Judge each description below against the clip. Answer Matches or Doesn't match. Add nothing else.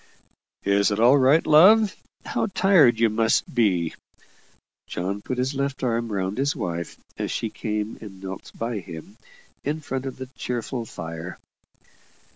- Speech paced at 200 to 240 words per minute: Doesn't match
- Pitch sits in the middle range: Doesn't match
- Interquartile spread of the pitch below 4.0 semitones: Doesn't match